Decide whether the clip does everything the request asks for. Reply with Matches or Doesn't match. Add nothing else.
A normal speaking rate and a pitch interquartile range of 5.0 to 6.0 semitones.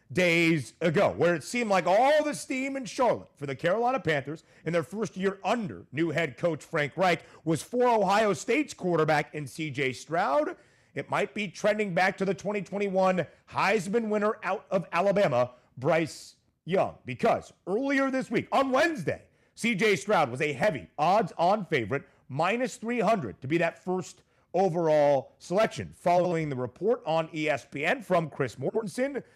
Matches